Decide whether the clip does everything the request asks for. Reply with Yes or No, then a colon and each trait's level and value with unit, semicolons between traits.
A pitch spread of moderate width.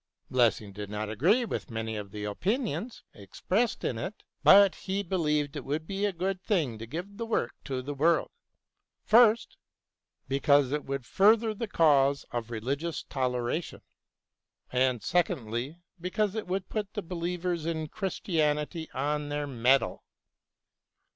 No: wide, 7.0 semitones